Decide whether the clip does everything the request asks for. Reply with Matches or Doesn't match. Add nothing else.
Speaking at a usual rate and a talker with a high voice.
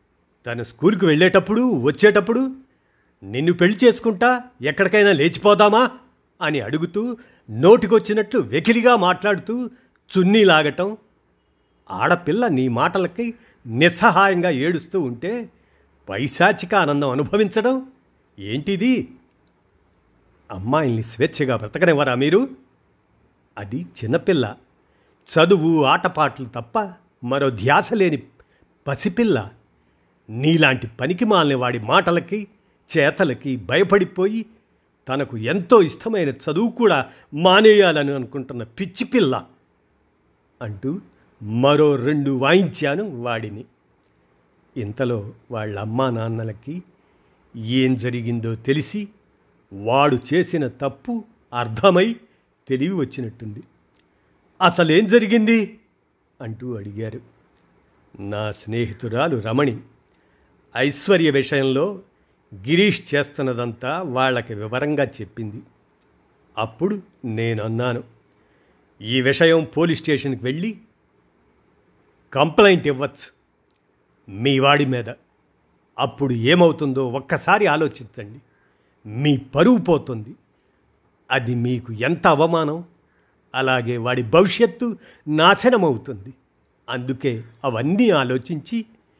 Doesn't match